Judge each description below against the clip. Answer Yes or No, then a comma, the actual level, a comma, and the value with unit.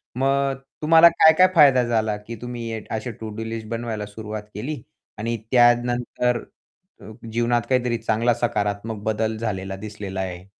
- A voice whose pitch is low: Yes, low, 115 Hz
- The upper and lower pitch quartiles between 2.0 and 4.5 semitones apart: Yes, narrow, 2.4 semitones